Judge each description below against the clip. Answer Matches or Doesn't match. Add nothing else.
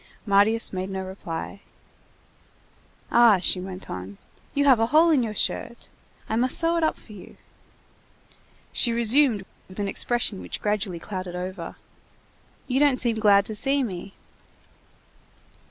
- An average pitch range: Matches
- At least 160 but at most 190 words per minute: Doesn't match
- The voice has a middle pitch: Doesn't match